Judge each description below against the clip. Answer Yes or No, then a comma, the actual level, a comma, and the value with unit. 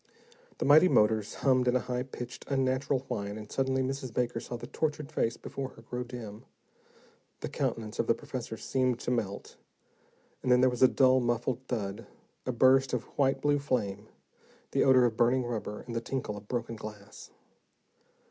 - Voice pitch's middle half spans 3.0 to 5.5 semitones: No, narrow, 2.6 semitones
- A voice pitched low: Yes, low, 125 Hz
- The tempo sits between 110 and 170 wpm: No, average, 180 wpm